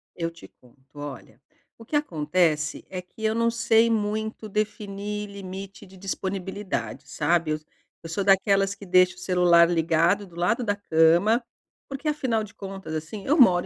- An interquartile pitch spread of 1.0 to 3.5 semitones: No, average, 3.9 semitones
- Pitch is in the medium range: No, high, 195 Hz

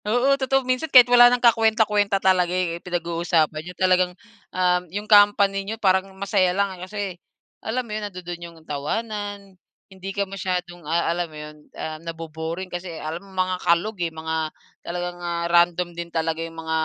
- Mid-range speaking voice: Yes, medium, 180 Hz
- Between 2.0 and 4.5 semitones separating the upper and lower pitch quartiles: Yes, average, 3.2 semitones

